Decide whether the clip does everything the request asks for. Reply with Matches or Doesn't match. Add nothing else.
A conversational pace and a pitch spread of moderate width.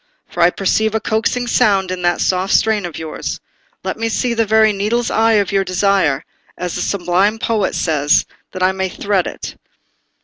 Matches